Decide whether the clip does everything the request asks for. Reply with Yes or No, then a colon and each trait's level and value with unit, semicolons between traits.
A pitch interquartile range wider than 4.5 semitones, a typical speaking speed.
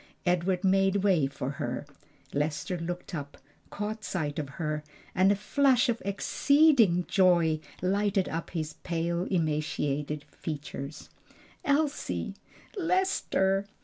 No: average, 4.9 semitones; slow, 115 wpm